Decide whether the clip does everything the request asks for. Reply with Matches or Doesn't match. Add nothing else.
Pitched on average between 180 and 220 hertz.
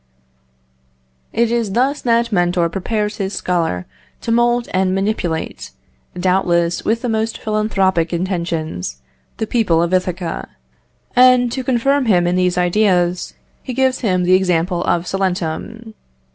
Matches